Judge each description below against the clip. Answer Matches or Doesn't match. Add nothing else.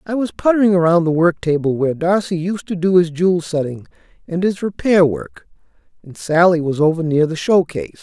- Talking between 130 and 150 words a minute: Doesn't match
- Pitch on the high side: Doesn't match